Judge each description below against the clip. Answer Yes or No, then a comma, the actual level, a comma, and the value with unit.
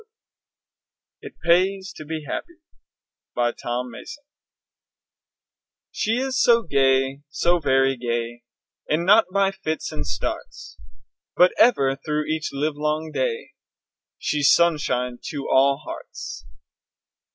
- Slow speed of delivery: Yes, slow, 110 wpm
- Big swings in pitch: Yes, wide, 6.0 semitones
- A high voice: No, medium, 150 Hz